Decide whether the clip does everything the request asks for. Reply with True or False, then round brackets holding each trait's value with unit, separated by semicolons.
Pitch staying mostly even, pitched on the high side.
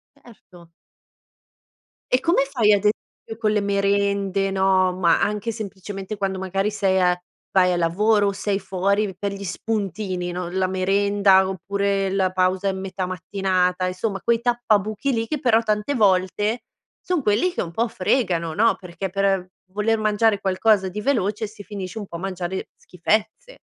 True (2.3 semitones; 200 Hz)